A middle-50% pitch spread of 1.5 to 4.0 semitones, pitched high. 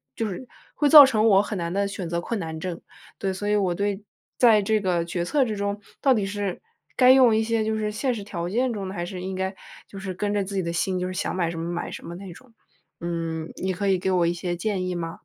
Yes: average, 3.3 semitones; high, 195 Hz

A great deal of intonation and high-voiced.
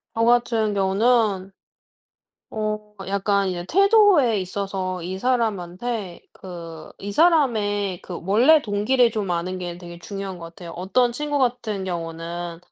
No: average, 4.6 semitones; high, 200 Hz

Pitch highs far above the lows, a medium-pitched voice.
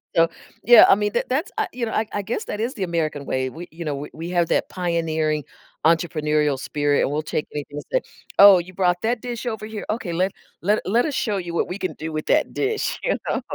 Yes: wide, 5.9 semitones; medium, 180 Hz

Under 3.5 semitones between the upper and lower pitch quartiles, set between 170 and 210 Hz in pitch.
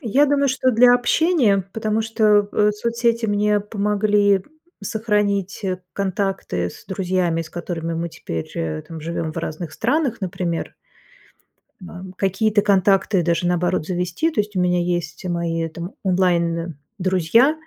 No: average, 3.8 semitones; high, 190 Hz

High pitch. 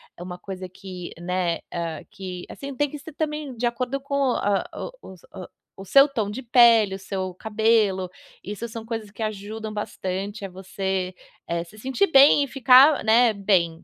Yes: high, 210 Hz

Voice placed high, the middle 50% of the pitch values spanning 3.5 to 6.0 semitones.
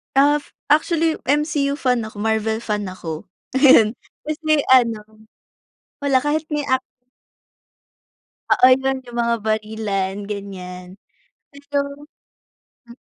Yes: high, 240 Hz; average, 5.0 semitones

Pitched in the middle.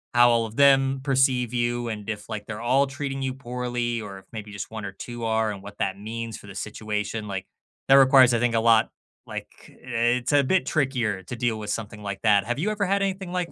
No: low, 120 Hz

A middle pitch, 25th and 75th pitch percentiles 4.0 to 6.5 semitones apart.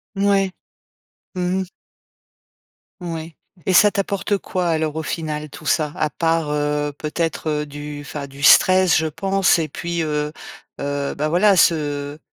No: medium, 160 Hz; average, 3.4 semitones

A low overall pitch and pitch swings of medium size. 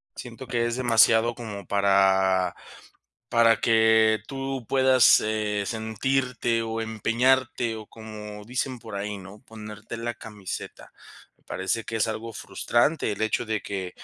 No: low, 110 Hz; narrow, 2.2 semitones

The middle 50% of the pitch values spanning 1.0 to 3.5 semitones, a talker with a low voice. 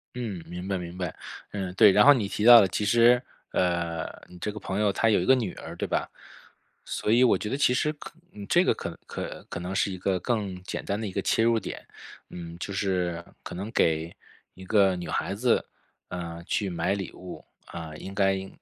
Yes: average, 3.2 semitones; very low, 95 Hz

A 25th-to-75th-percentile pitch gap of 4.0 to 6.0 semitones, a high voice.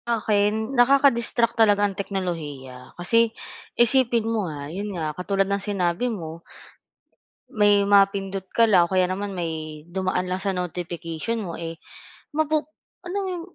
Yes: average, 4.5 semitones; high, 195 Hz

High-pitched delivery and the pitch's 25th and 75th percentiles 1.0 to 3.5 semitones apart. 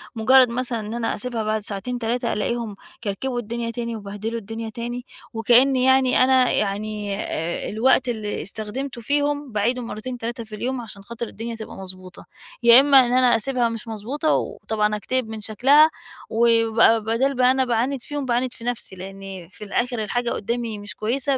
Yes: high, 235 Hz; average, 2.8 semitones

